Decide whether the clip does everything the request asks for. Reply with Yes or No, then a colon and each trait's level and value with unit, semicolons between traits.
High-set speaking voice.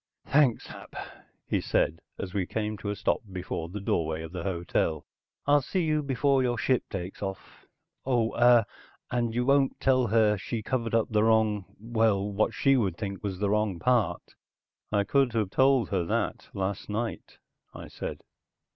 No: low, 110 Hz